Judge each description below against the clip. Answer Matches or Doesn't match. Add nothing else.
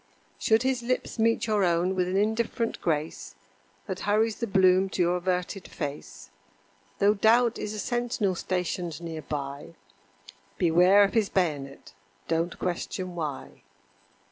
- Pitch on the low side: Doesn't match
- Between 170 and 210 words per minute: Doesn't match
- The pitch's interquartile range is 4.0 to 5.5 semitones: Matches